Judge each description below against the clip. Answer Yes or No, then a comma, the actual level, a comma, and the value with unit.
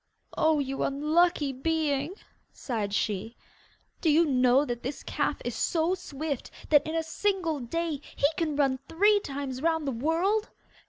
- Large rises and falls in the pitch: No, average, 3.5 semitones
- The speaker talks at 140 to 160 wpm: Yes, average, 155 wpm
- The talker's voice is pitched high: Yes, very high, 295 Hz